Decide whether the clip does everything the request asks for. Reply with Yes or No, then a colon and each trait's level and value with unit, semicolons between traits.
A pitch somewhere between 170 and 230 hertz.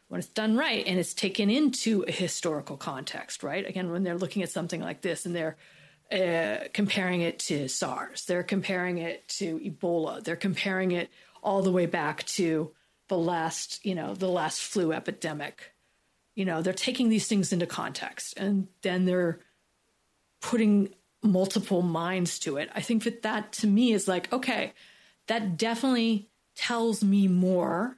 Yes: medium, 185 Hz